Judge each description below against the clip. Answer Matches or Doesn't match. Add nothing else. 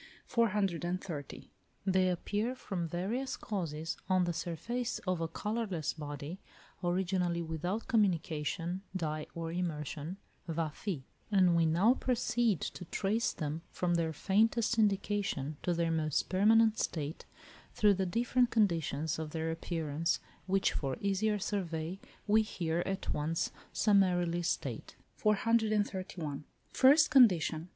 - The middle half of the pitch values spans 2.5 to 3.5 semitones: Doesn't match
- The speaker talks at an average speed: Doesn't match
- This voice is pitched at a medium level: Matches